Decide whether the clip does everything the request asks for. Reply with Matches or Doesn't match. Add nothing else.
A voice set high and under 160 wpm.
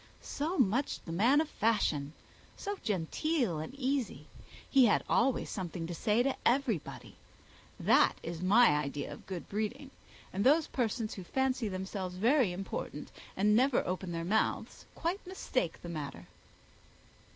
Matches